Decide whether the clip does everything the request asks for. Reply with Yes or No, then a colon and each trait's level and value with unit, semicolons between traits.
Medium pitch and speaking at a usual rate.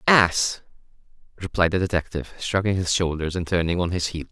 No: very low, 90 Hz; average, 165 wpm